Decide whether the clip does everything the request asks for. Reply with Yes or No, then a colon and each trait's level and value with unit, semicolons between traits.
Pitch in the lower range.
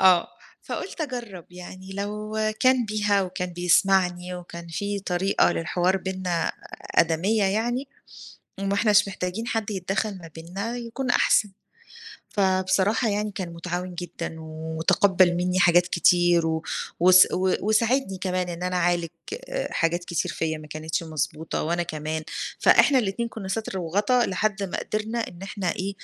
No: medium, 185 Hz